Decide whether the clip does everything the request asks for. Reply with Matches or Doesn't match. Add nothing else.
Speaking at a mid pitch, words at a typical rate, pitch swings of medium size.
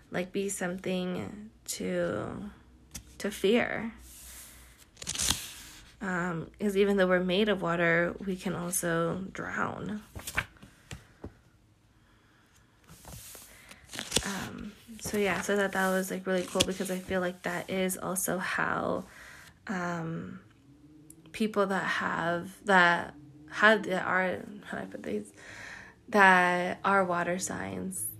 Doesn't match